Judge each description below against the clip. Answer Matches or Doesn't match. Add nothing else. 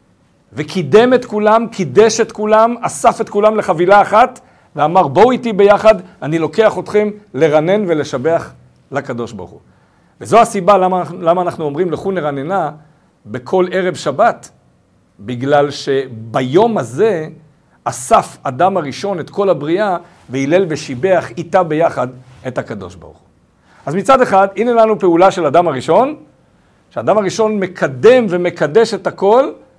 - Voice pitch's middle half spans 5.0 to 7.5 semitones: Matches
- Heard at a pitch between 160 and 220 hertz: Matches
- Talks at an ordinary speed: Matches